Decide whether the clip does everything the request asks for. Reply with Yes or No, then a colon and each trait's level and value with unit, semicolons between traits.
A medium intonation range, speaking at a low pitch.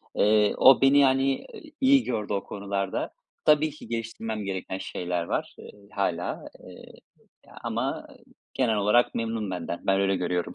Yes: average, 5.0 semitones; low, 105 Hz